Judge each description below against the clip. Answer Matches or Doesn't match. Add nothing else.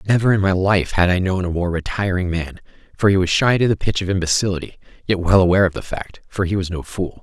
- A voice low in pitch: Matches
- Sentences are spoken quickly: Matches